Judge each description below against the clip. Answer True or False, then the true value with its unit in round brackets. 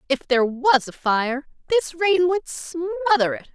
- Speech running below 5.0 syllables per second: True (4.7 syllables/s)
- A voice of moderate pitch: False (300 Hz)